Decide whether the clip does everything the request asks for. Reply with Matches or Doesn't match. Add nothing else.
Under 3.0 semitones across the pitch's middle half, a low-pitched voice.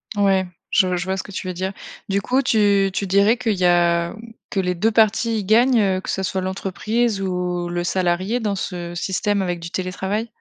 Doesn't match